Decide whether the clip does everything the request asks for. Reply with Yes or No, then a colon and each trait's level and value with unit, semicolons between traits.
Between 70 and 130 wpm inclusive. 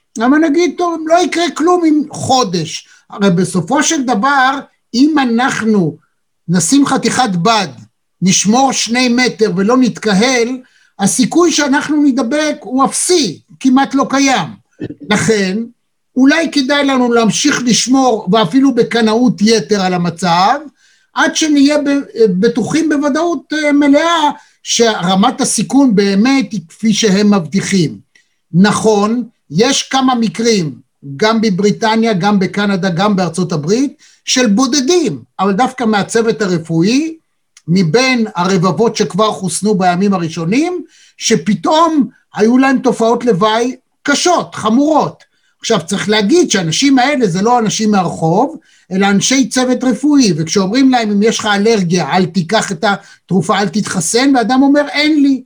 Yes: average, 120 wpm